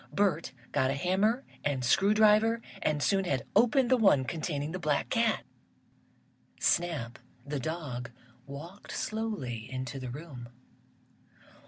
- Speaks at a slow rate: Yes, slow, 130 wpm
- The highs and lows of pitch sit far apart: Yes, wide, 7.8 semitones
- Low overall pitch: No, medium, 160 Hz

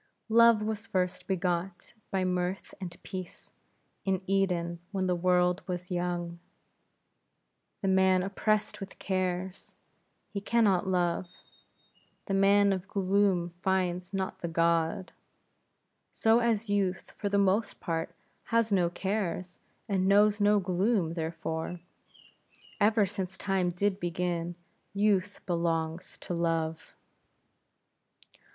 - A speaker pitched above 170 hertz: Yes, medium, 185 Hz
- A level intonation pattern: Yes, narrow, 2.3 semitones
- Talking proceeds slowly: Yes, slow, 120 wpm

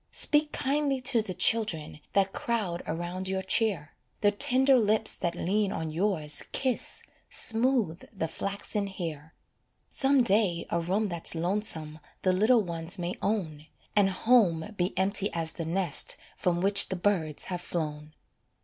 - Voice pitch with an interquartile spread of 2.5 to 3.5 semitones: No, average, 4.5 semitones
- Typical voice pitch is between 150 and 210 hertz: Yes, high, 190 Hz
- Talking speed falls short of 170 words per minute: Yes, average, 150 wpm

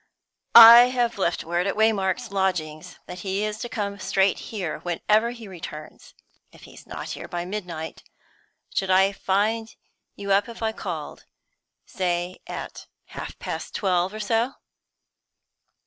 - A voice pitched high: Yes, high, 195 Hz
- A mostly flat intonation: No, average, 3.6 semitones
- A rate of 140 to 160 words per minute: Yes, average, 145 wpm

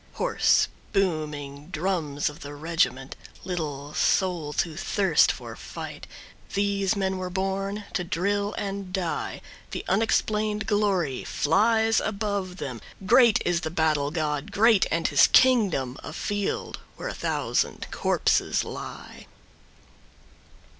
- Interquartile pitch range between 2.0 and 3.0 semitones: No, average, 4.8 semitones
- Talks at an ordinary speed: No, slow, 120 wpm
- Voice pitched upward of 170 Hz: Yes, medium, 185 Hz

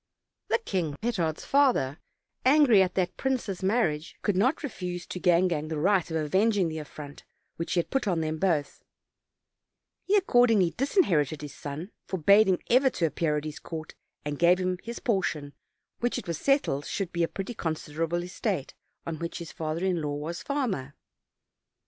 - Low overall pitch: No, medium, 175 Hz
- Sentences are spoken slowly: No, average, 180 wpm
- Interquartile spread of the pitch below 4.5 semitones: No, wide, 5.5 semitones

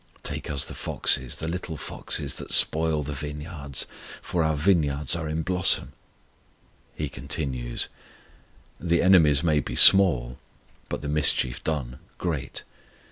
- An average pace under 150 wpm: Yes, slow, 135 wpm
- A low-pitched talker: Yes, very low, 75 Hz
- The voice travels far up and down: No, average, 2.9 semitones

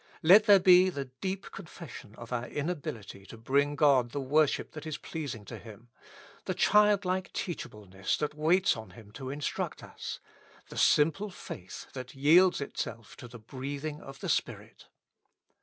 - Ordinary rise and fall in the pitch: No, wide, 6.4 semitones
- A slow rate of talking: No, average, 160 wpm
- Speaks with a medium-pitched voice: Yes, medium, 145 Hz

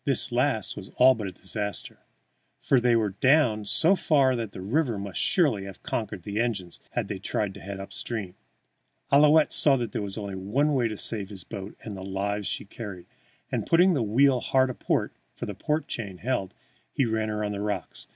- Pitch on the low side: Yes, low, 110 Hz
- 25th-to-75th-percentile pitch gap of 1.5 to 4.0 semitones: No, average, 4.7 semitones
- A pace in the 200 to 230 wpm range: Yes, fast, 205 wpm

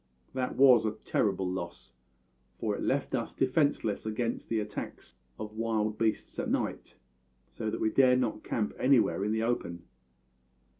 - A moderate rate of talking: Yes, average, 155 wpm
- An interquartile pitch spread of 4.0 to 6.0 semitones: No, average, 2.9 semitones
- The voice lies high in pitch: No, low, 110 Hz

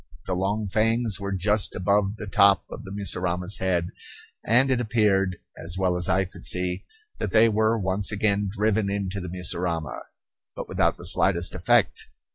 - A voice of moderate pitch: No, very low, 95 Hz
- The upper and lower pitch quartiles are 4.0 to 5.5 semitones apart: No, narrow, 2.6 semitones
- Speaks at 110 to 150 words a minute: No, average, 170 wpm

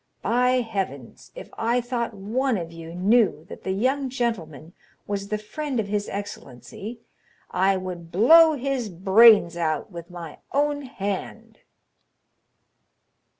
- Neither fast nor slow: No, slow, 130 wpm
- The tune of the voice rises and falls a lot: Yes, wide, 5.7 semitones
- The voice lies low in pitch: No, high, 205 Hz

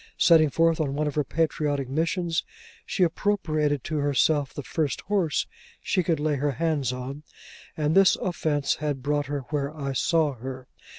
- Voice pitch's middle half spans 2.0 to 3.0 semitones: Yes, narrow, 2.5 semitones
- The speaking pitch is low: No, medium, 150 Hz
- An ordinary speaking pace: Yes, average, 170 wpm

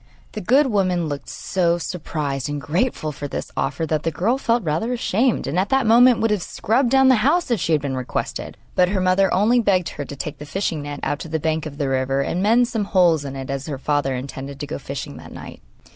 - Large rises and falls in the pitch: Yes, wide, 7.1 semitones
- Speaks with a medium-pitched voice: Yes, medium, 170 Hz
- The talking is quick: Yes, fast, 245 wpm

